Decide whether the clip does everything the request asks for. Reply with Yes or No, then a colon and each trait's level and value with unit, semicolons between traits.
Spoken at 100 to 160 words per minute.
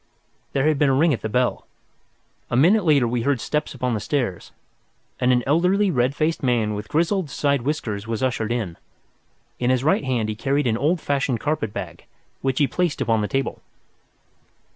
No: average, 190 wpm